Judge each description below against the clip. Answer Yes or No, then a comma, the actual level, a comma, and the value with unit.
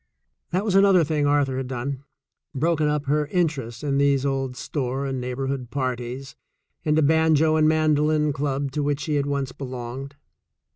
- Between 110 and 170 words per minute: No, average, 180 wpm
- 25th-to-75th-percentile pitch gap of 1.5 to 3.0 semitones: Yes, narrow, 2.4 semitones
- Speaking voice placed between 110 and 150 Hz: Yes, medium, 140 Hz